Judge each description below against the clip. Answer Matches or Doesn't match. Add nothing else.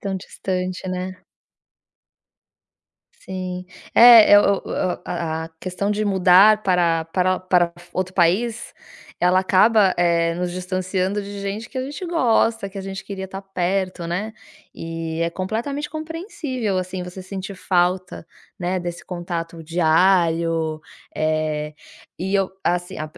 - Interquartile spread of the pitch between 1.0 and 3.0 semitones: Matches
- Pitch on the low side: Doesn't match